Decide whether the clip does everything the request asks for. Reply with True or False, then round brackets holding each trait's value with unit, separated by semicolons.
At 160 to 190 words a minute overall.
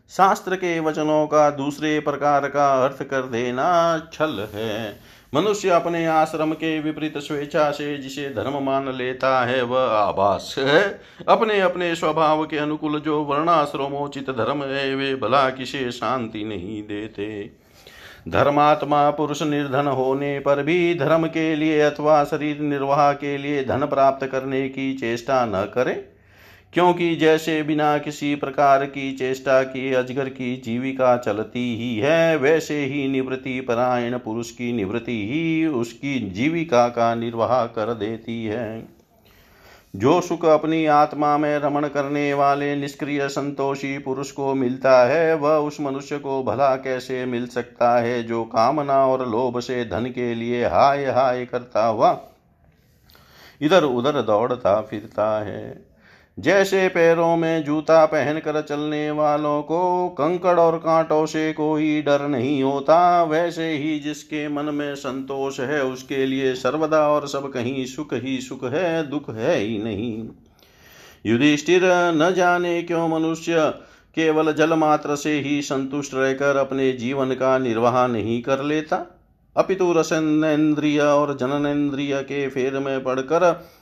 False (140 wpm)